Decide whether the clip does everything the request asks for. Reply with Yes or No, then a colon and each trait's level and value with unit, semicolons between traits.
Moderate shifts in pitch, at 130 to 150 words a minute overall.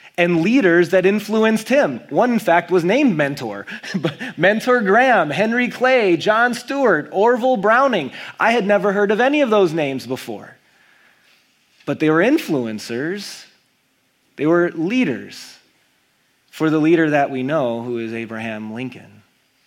No: wide, 8.2 semitones; average, 140 wpm